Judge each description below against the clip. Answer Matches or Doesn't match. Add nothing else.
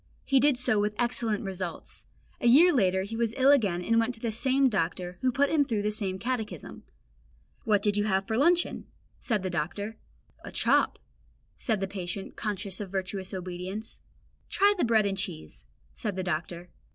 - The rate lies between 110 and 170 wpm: Doesn't match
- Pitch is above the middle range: Matches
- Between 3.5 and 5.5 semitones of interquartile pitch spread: Matches